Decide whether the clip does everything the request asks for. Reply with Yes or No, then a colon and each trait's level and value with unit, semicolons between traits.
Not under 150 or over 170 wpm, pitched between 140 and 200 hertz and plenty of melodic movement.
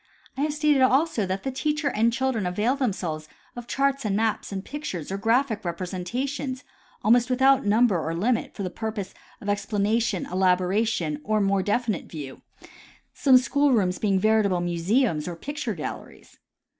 No: average, 165 wpm; high, 215 Hz; wide, 5.7 semitones